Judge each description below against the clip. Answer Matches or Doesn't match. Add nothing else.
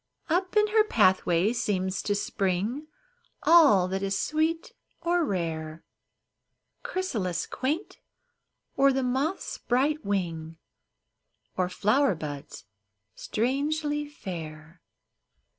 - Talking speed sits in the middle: Doesn't match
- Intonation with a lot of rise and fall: Matches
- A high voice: Matches